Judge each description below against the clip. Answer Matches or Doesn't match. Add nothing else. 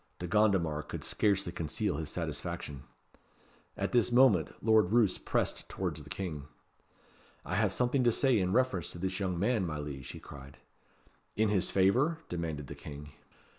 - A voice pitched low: Matches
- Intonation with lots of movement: Matches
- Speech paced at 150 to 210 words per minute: Matches